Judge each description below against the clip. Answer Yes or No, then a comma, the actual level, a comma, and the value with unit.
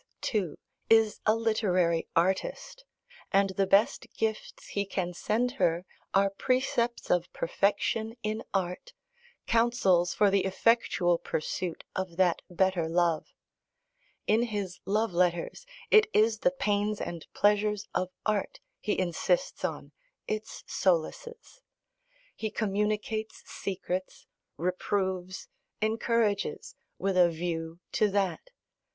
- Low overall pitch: No, high, 200 Hz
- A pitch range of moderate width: Yes, average, 3.5 semitones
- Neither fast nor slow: No, slow, 115 wpm